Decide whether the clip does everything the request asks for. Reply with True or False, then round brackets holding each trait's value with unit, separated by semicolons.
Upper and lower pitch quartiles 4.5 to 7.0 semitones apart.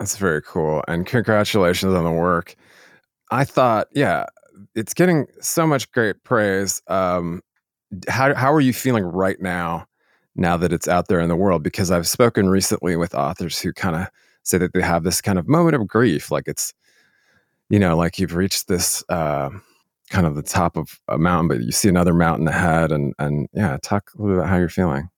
False (3.7 semitones)